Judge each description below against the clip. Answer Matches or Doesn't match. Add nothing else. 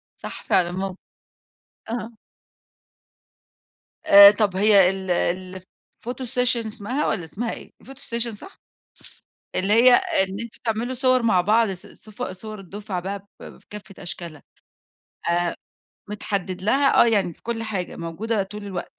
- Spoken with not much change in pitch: Doesn't match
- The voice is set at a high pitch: Matches